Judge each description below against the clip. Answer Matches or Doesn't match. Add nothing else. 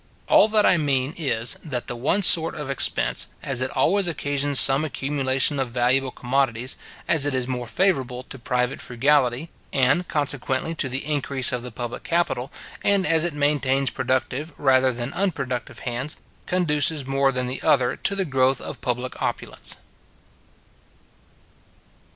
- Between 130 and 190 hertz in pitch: Matches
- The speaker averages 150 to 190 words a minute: Matches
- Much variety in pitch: Doesn't match